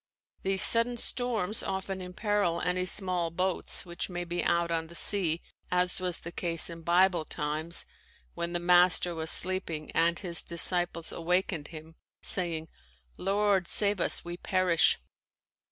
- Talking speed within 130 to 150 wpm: Yes, average, 145 wpm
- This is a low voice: No, medium, 175 Hz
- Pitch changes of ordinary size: No, narrow, 1.9 semitones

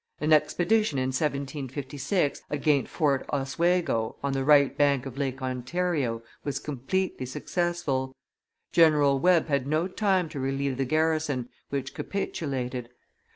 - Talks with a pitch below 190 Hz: Yes, medium, 140 Hz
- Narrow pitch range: No, average, 3.3 semitones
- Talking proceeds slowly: Yes, slow, 125 wpm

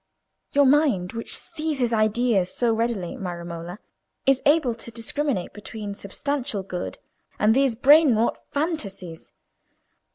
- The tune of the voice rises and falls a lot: Yes, wide, 6.0 semitones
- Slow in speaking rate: Yes, slow, 125 wpm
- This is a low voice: No, high, 230 Hz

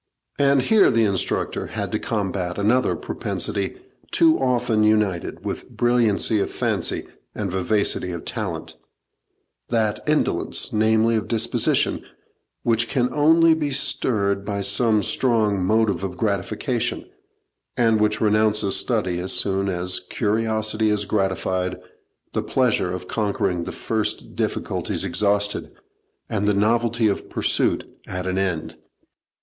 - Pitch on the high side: No, low, 105 Hz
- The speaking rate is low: Yes, slow, 125 wpm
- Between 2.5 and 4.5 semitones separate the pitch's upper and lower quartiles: Yes, average, 2.8 semitones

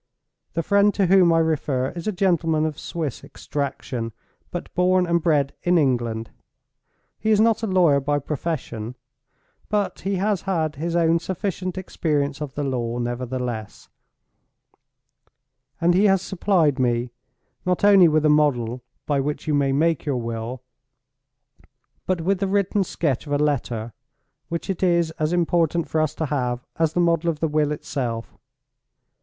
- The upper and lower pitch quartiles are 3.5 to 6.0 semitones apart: Yes, average, 4.9 semitones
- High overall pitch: No, medium, 155 Hz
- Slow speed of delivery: No, average, 160 wpm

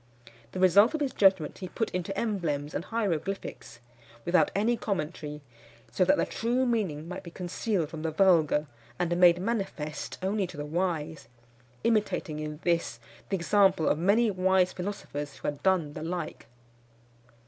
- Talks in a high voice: No, medium, 180 Hz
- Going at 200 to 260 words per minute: No, average, 160 wpm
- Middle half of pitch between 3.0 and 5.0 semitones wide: Yes, average, 4.4 semitones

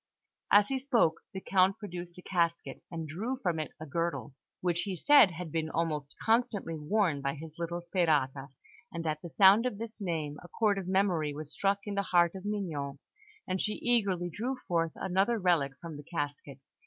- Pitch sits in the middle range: Yes, medium, 175 Hz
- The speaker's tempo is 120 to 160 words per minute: No, average, 190 wpm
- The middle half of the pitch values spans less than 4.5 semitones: Yes, average, 4.1 semitones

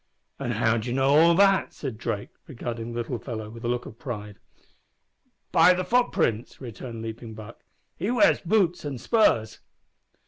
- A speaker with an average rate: Yes, average, 165 wpm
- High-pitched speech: No, low, 120 Hz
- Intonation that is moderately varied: No, wide, 6.9 semitones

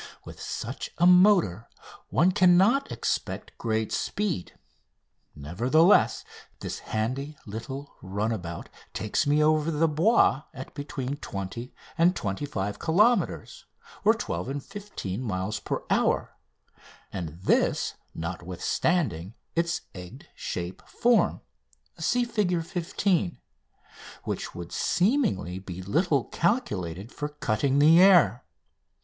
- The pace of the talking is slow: Yes, slow, 105 wpm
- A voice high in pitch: No, medium, 140 Hz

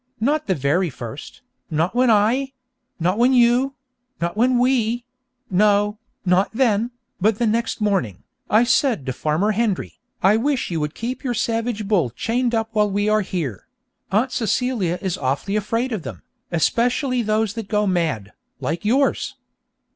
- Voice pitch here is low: No, high, 215 Hz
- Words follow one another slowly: No, average, 160 wpm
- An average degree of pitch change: Yes, average, 4.8 semitones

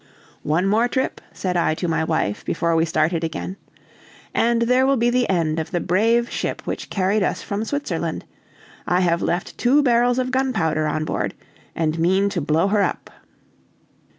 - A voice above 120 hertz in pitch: Yes, medium, 185 Hz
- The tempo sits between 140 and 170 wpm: No, average, 180 wpm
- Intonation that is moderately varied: No, wide, 6.5 semitones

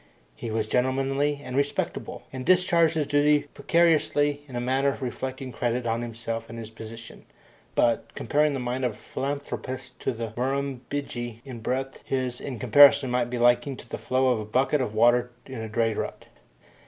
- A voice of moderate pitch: No, low, 130 Hz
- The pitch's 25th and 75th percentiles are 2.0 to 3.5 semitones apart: Yes, average, 2.9 semitones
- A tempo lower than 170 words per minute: No, average, 180 wpm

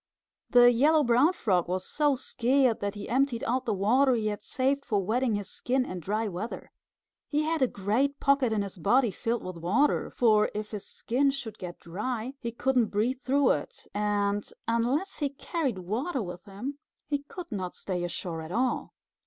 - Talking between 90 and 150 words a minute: No, average, 185 wpm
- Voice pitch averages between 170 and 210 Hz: No, high, 235 Hz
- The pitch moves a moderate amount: Yes, average, 4.9 semitones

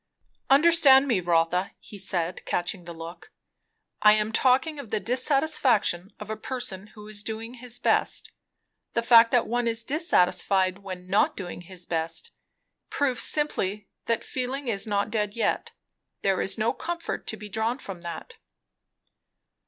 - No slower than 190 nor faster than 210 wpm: No, average, 150 wpm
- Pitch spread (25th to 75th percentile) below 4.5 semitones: No, average, 5.0 semitones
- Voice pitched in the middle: No, high, 215 Hz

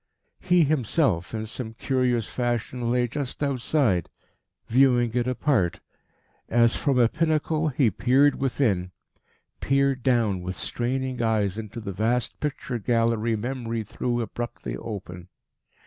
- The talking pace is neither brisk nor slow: No, slow, 125 wpm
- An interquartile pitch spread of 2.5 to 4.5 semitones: Yes, average, 3.3 semitones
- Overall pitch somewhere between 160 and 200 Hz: No, low, 120 Hz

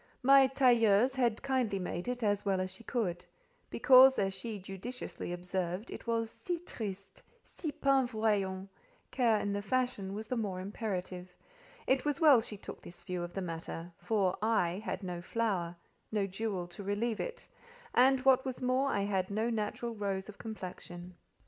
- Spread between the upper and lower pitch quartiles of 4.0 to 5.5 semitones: Yes, average, 4.7 semitones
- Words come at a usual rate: Yes, average, 170 wpm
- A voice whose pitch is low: No, high, 210 Hz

